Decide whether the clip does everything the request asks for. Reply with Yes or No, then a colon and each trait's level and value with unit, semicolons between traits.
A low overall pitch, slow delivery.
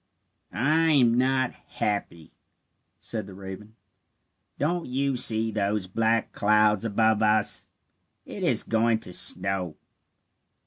Yes: low, 110 Hz; slow, 115 wpm